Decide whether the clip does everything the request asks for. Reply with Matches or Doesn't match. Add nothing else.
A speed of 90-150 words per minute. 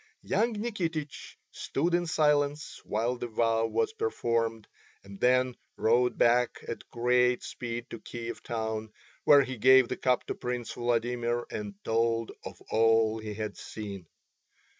Matches